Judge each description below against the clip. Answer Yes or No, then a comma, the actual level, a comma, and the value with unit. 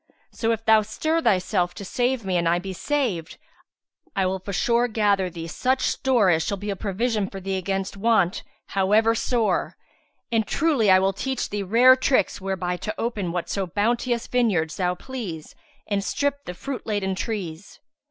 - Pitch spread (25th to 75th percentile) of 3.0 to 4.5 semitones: Yes, average, 4.0 semitones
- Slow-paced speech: No, average, 170 wpm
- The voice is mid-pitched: No, high, 205 Hz